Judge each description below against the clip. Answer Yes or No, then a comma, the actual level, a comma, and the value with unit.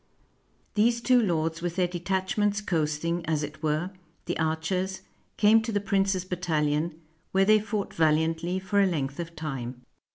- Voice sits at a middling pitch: Yes, medium, 175 Hz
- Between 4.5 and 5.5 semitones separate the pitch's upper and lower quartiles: No, average, 3.7 semitones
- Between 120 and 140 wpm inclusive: No, average, 160 wpm